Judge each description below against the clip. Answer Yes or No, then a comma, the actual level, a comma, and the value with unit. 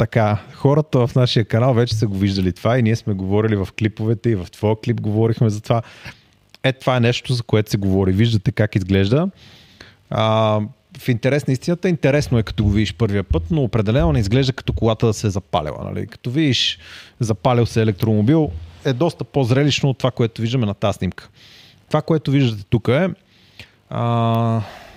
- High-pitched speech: No, low, 115 Hz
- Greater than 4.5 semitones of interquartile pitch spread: No, average, 3.7 semitones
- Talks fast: Yes, fast, 185 wpm